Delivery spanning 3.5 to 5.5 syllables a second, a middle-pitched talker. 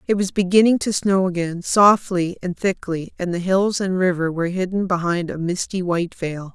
Yes: 5.1 syllables/s; medium, 180 Hz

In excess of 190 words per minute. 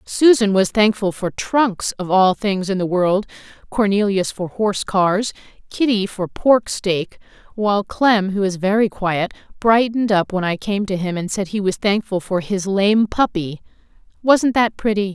No: average, 175 wpm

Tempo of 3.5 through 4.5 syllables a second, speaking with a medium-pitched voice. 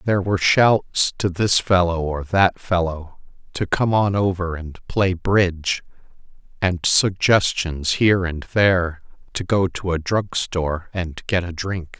No: 4.1 syllables/s; very low, 90 Hz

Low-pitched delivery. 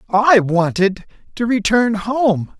No: high, 215 Hz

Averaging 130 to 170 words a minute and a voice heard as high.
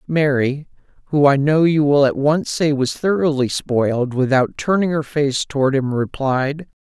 No: average, 165 wpm; medium, 145 Hz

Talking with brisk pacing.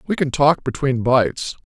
No: average, 180 wpm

